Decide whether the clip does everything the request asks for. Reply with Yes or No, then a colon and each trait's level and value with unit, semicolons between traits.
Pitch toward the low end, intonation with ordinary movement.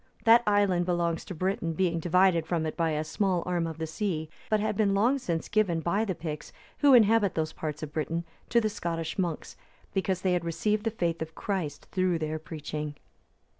No: medium, 175 Hz; average, 3.9 semitones